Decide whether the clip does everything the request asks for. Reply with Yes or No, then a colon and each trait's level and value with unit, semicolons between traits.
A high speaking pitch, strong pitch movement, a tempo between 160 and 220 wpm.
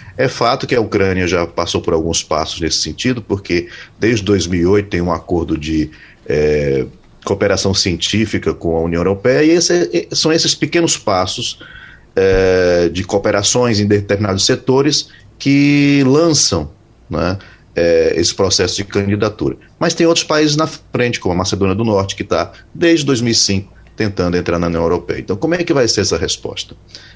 No: low, 100 Hz; wide, 6.2 semitones; average, 165 wpm